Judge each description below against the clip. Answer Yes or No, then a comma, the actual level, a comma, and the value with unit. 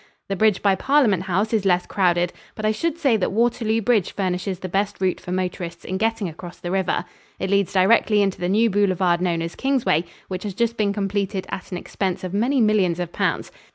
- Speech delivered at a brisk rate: Yes, fast, 215 wpm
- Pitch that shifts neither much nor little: Yes, average, 3.1 semitones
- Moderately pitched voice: No, high, 195 Hz